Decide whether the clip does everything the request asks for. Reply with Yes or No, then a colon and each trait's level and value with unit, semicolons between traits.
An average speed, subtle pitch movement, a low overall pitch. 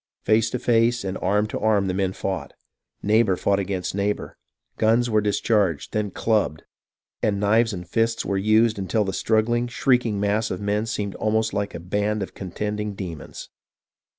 Yes: average, 175 wpm; narrow, 2.2 semitones; low, 105 Hz